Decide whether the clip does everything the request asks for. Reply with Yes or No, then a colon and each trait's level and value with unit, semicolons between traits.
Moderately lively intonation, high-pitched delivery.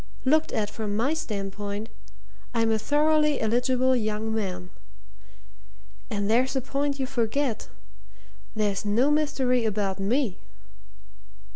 Yes: average, 4.4 semitones; high, 230 Hz